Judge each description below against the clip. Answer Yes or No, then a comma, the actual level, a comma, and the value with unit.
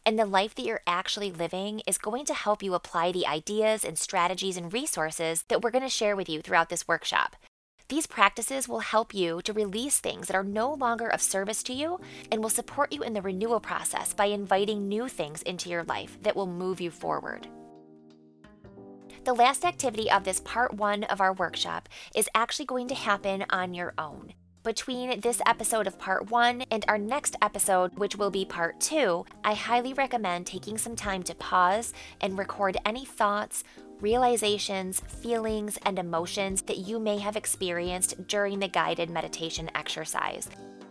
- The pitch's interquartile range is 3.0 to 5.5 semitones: Yes, average, 4.3 semitones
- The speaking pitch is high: Yes, high, 200 Hz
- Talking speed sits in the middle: Yes, average, 180 wpm